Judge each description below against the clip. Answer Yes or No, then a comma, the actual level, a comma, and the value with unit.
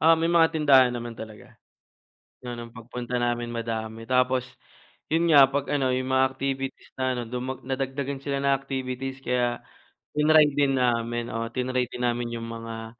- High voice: No, low, 125 Hz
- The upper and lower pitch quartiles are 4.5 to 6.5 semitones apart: No, narrow, 2.4 semitones